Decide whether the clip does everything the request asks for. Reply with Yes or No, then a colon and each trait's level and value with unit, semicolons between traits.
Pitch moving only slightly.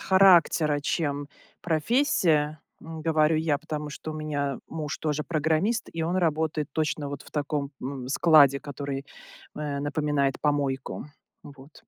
Yes: narrow, 2.0 semitones